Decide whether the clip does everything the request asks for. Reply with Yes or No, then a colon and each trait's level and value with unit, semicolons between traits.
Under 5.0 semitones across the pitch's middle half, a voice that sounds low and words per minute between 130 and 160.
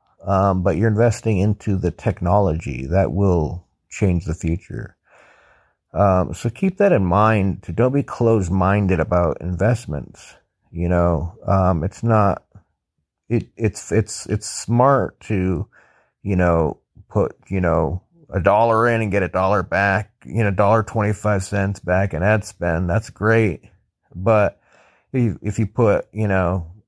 Yes: average, 3.4 semitones; low, 100 Hz; average, 150 wpm